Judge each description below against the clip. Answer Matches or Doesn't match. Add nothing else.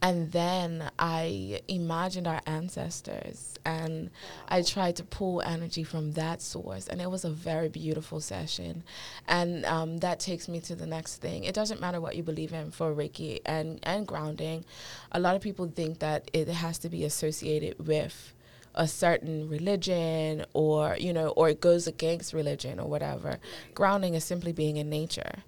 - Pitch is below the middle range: Doesn't match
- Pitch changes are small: Matches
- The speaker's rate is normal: Matches